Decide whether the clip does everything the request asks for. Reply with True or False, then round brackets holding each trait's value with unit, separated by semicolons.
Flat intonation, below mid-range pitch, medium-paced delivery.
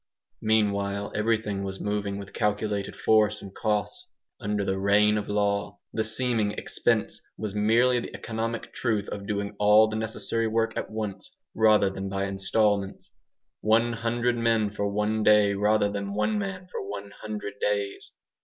True (1.6 semitones; 105 Hz; 155 wpm)